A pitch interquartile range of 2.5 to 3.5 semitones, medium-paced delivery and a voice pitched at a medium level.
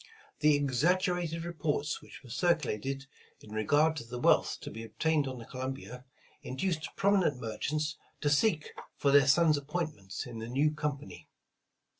No: average, 3.9 semitones; average, 160 wpm; medium, 145 Hz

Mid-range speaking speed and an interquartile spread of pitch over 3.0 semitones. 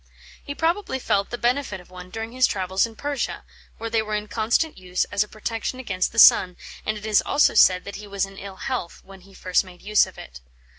No: fast, 235 wpm; average, 3.9 semitones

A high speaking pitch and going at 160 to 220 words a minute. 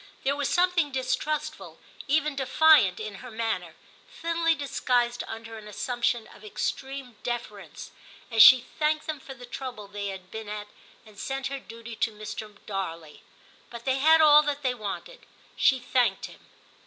Yes: high, 245 Hz; average, 165 wpm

